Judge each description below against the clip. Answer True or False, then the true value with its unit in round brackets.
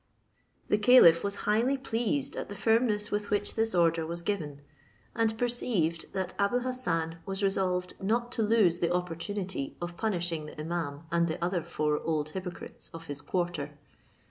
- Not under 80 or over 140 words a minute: False (165 wpm)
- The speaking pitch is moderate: True (180 Hz)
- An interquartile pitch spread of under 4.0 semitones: False (4.3 semitones)